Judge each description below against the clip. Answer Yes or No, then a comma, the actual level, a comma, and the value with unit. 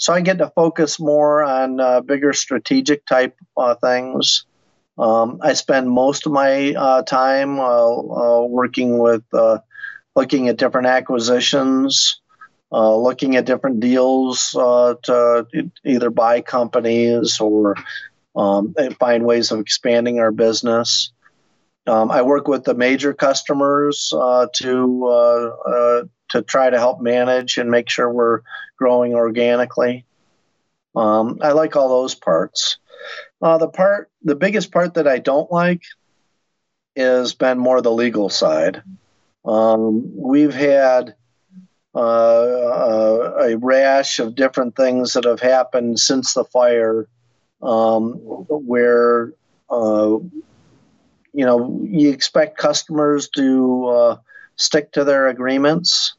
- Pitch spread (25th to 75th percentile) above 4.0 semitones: No, average, 3.1 semitones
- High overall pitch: No, low, 125 Hz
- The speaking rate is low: Yes, slow, 130 wpm